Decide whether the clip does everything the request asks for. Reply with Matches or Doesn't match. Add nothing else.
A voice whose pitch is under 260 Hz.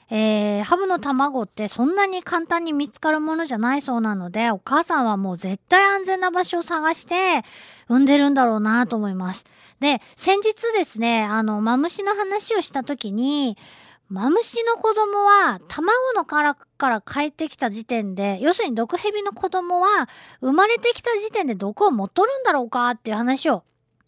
Doesn't match